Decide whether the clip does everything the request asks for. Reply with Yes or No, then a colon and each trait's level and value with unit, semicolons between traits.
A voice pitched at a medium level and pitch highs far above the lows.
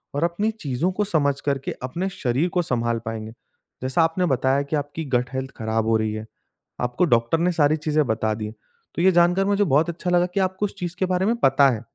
Yes: medium, 150 Hz; wide, 6.4 semitones